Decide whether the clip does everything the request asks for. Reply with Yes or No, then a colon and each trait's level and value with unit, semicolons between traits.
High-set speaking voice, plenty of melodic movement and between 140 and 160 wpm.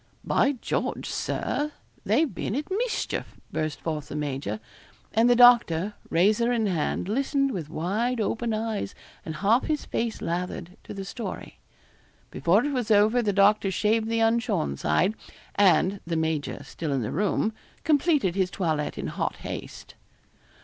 Yes: high, 210 Hz; wide, 6.0 semitones; average, 155 wpm